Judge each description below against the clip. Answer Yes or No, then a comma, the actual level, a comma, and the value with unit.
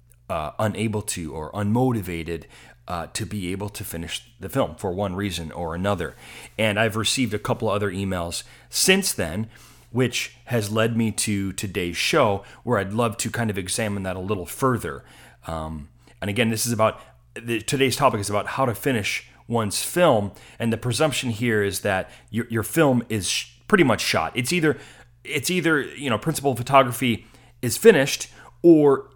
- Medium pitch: No, low, 110 Hz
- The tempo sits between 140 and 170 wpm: No, average, 180 wpm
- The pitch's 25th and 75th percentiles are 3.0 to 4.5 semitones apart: Yes, average, 4.0 semitones